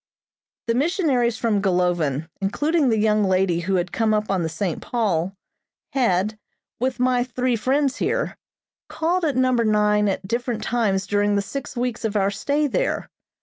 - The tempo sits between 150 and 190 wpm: Yes, average, 165 wpm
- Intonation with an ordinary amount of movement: Yes, average, 4.6 semitones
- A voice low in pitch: No, high, 215 Hz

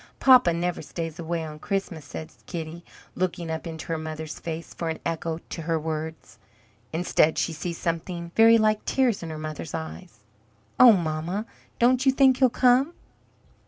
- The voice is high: No, medium, 170 Hz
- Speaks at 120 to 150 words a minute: No, average, 165 wpm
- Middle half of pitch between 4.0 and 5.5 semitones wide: Yes, average, 4.6 semitones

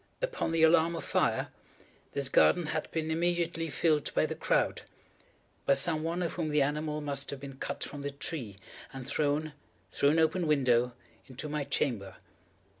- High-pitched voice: No, medium, 150 Hz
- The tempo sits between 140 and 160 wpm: No, average, 170 wpm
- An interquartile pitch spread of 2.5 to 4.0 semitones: Yes, average, 2.8 semitones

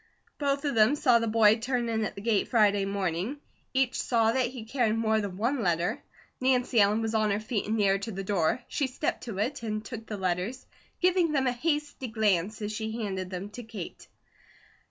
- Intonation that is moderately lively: Yes, average, 3.6 semitones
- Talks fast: Yes, fast, 210 wpm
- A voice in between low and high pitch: No, high, 220 Hz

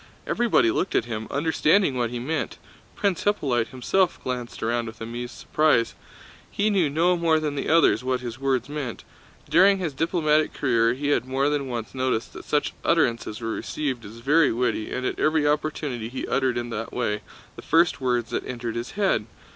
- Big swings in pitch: No, average, 4.8 semitones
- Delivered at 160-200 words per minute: Yes, average, 185 wpm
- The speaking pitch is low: Yes, low, 130 Hz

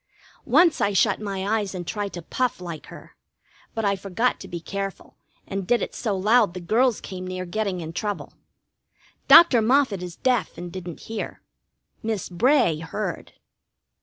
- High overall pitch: Yes, high, 200 Hz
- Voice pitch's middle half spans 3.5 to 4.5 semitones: Yes, average, 3.8 semitones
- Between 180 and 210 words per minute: No, average, 165 wpm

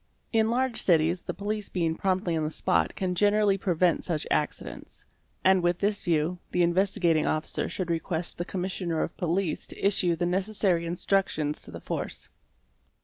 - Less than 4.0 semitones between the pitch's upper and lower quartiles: Yes, average, 2.8 semitones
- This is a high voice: No, medium, 180 Hz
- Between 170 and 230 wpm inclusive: Yes, average, 175 wpm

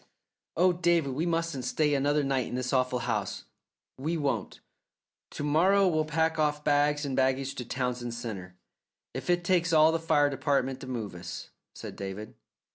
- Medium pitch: Yes, medium, 145 Hz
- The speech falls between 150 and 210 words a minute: Yes, average, 170 wpm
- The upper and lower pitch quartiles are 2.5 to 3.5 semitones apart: No, average, 4.3 semitones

